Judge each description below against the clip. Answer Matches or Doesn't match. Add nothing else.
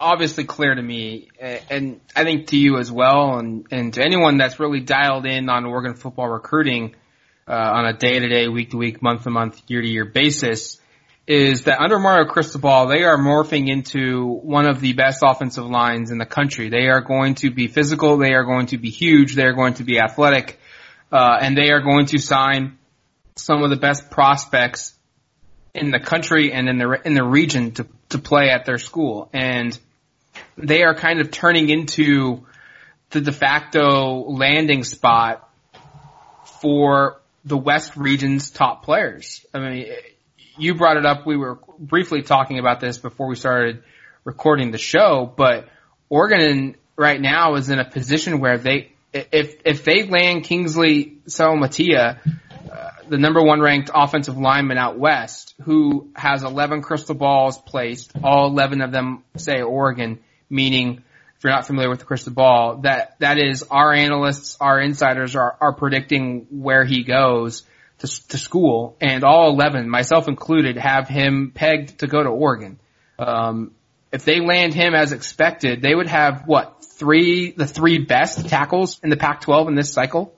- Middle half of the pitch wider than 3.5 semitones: Doesn't match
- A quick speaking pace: Doesn't match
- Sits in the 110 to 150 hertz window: Matches